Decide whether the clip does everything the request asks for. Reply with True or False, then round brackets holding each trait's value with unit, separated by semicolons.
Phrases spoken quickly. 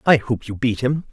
True (270 wpm)